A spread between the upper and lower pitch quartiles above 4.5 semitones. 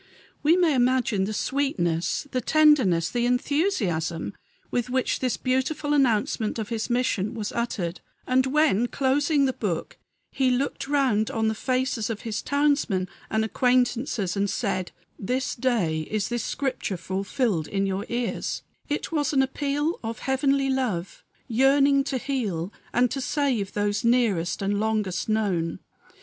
Yes: average, 4.9 semitones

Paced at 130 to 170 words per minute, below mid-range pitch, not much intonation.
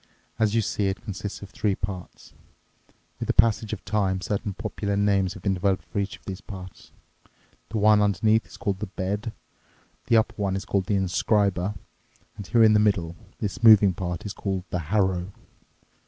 No: average, 185 wpm; low, 100 Hz; narrow, 2.0 semitones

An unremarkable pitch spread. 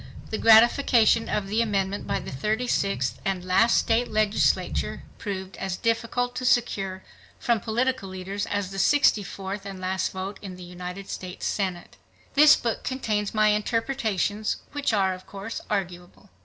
Yes: average, 3.2 semitones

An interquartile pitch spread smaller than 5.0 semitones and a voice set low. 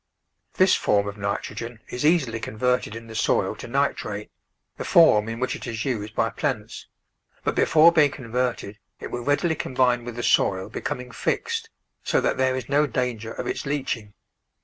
Yes: average, 4.1 semitones; low, 125 Hz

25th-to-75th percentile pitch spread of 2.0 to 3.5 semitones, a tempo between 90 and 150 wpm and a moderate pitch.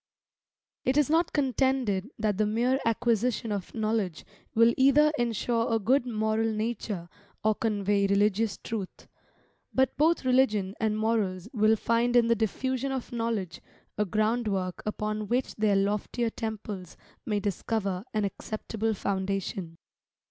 No: average, 2.8 semitones; slow, 135 wpm; high, 220 Hz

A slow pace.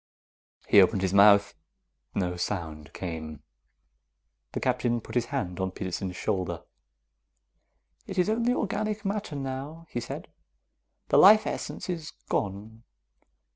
Yes: slow, 125 wpm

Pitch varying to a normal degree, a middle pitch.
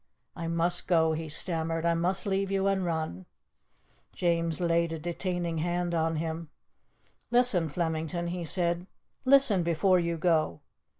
No: narrow, 1.6 semitones; medium, 170 Hz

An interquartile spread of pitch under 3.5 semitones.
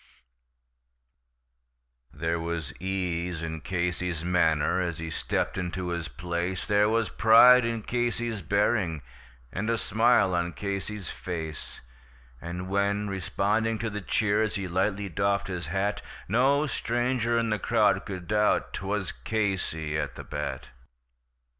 No: average, 3.9 semitones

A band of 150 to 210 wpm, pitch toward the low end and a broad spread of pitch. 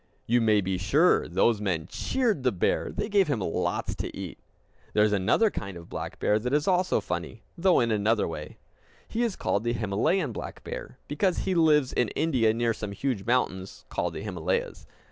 Yes: average, 195 wpm; low, 115 Hz; wide, 8.3 semitones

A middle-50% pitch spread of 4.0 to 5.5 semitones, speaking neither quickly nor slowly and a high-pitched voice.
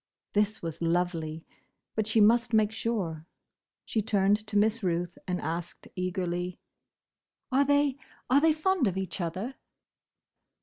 No: average, 4.7 semitones; slow, 125 wpm; high, 205 Hz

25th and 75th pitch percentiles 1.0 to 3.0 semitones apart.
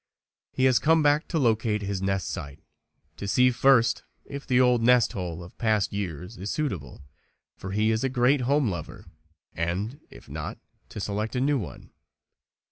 No: average, 5.0 semitones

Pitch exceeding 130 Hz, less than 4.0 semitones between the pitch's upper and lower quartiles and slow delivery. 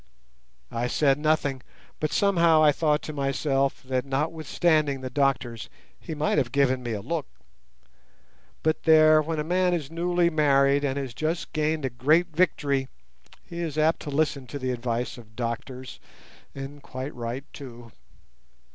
No: medium, 140 Hz; average, 3.2 semitones; average, 155 wpm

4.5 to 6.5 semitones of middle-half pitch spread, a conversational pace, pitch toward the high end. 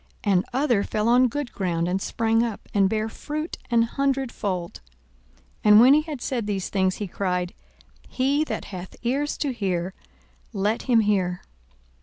Yes: average, 5.1 semitones; average, 165 wpm; high, 220 Hz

